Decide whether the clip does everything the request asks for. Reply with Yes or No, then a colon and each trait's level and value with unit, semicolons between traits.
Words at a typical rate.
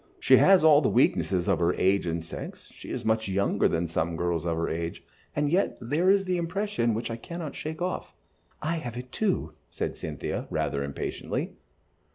Yes: average, 195 wpm